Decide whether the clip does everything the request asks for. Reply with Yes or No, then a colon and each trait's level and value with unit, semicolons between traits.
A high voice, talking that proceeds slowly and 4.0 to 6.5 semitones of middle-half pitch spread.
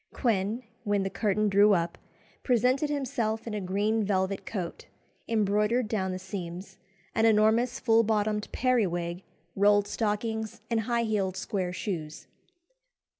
No: high, 210 Hz; slow, 130 wpm; average, 2.8 semitones